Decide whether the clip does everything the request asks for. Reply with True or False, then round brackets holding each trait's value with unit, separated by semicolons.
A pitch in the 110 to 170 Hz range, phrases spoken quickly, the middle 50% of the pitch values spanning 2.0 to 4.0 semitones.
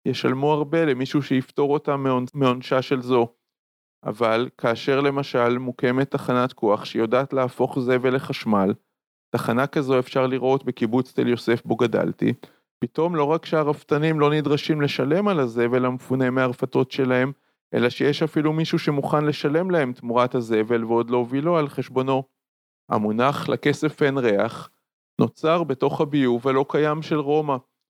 False (135 Hz; 135 wpm; 3.0 semitones)